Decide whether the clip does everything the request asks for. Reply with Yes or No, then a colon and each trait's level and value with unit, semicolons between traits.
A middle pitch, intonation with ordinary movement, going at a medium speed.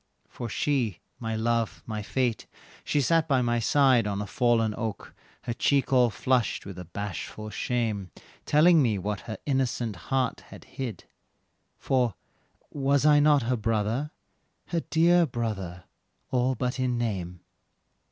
No: low, 120 Hz; average, 3.9 semitones; average, 145 wpm